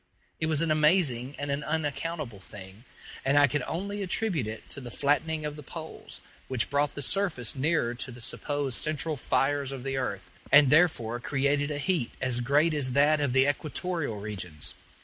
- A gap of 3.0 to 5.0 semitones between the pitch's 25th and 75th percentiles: Yes, average, 3.9 semitones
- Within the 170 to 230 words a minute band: Yes, average, 185 wpm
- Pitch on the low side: No, medium, 145 Hz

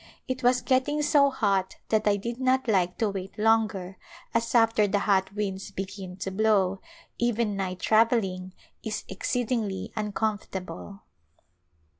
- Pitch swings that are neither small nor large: Yes, average, 3.3 semitones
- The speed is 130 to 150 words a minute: Yes, average, 140 wpm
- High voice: Yes, high, 210 Hz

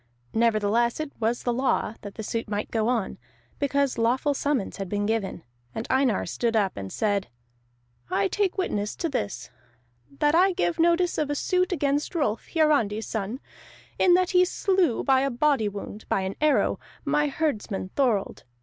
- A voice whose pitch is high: Yes, high, 245 Hz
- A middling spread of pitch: No, wide, 6.2 semitones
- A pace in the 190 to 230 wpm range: No, average, 170 wpm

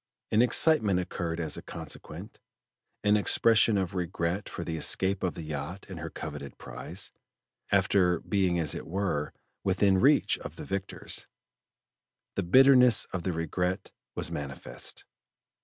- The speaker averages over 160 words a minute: No, average, 140 wpm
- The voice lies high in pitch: No, very low, 90 Hz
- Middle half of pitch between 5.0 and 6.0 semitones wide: No, average, 3.5 semitones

